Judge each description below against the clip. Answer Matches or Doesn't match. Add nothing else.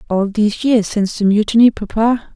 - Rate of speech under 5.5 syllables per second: Doesn't match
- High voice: Matches